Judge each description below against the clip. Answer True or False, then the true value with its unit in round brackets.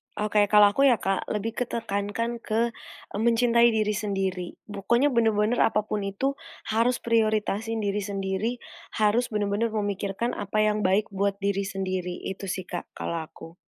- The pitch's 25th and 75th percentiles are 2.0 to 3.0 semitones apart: True (2.4 semitones)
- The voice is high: True (210 Hz)